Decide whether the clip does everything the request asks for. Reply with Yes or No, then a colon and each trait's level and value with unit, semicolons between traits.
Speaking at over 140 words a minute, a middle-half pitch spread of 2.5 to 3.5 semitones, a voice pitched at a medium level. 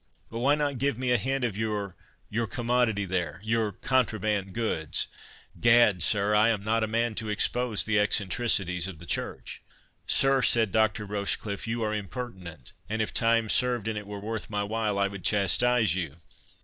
No: average, 175 wpm; average, 2.8 semitones; low, 110 Hz